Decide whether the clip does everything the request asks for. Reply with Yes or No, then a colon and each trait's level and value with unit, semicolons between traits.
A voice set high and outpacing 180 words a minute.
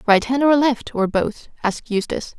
Yes: high, 235 Hz; average, 200 wpm